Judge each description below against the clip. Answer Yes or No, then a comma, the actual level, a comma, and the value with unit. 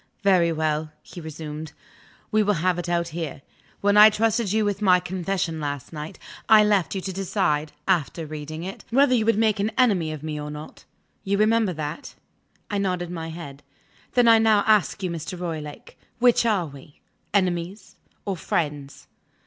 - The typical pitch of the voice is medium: Yes, medium, 180 Hz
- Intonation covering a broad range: No, average, 4.8 semitones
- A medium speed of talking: Yes, average, 175 wpm